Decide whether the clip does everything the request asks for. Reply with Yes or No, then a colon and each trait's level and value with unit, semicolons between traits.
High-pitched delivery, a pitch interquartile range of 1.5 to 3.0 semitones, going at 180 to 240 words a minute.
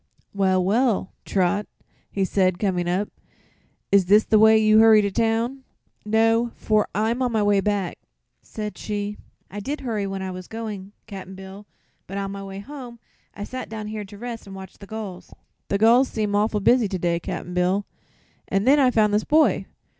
Yes: high, 210 Hz; narrow, 2.4 semitones; average, 190 wpm